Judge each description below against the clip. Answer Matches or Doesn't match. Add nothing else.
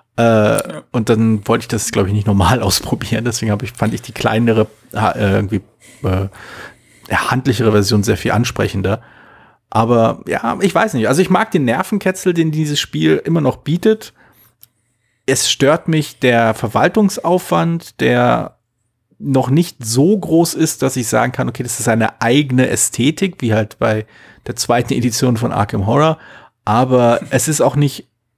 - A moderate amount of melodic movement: Matches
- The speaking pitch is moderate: Doesn't match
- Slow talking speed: Doesn't match